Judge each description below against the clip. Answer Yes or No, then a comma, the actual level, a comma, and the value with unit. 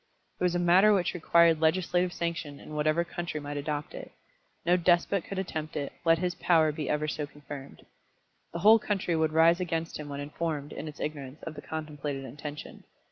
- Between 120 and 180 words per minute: No, average, 190 wpm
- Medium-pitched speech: Yes, medium, 160 Hz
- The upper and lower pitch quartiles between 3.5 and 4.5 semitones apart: No, average, 2.7 semitones